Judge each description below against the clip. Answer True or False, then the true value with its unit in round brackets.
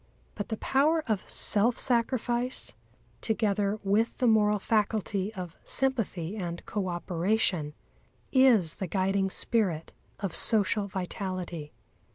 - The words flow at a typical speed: False (115 wpm)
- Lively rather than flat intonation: False (3.5 semitones)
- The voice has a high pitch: True (205 Hz)